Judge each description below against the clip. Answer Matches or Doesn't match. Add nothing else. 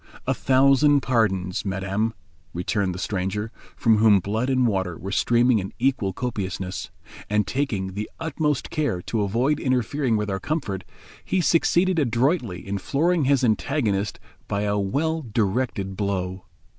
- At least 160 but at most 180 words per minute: Doesn't match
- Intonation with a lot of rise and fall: Matches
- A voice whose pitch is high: Doesn't match